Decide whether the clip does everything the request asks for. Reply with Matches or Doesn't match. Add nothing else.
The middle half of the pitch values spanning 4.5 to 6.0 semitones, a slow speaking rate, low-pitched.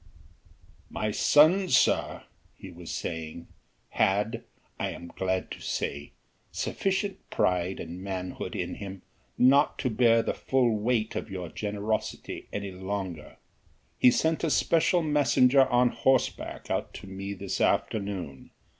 Matches